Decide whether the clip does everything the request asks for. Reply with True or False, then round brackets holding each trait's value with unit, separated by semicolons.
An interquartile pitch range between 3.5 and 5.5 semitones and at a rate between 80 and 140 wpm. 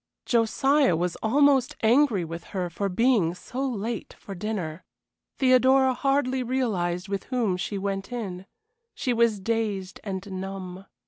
True (5.2 semitones; 135 wpm)